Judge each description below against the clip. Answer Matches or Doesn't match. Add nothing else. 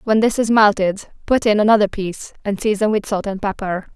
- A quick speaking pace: Matches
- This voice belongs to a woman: Matches